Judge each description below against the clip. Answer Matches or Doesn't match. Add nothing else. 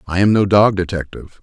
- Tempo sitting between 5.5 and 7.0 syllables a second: Matches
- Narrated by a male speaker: Matches